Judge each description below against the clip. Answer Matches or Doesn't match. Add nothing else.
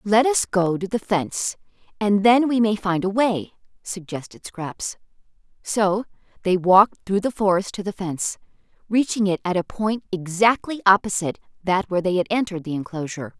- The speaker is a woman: Matches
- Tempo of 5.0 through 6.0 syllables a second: Matches